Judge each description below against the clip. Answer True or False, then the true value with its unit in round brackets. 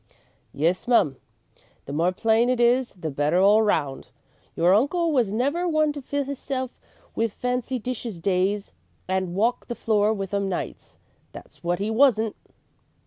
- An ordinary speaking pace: True (155 wpm)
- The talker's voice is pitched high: True (220 Hz)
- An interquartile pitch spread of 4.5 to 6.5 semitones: True (5.4 semitones)